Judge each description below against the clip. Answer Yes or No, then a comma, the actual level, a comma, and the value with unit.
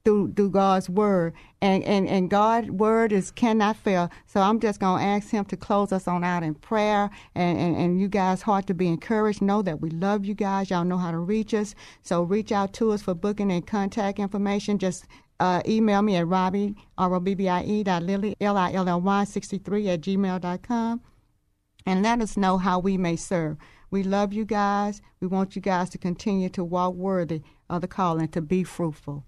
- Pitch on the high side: Yes, high, 195 Hz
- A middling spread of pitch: No, narrow, 2.3 semitones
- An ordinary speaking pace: No, fast, 220 wpm